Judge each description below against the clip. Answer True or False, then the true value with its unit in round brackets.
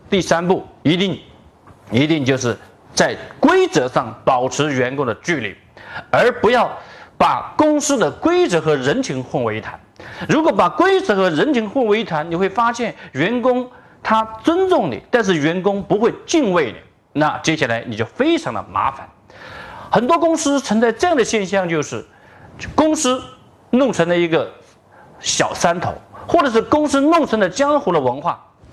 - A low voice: False (210 Hz)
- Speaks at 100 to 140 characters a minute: False (240 characters per minute)